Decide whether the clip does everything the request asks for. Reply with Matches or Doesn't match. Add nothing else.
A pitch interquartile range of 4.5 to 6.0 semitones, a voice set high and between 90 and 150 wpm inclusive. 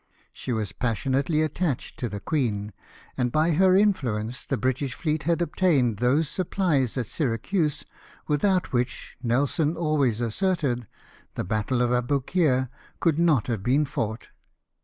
Doesn't match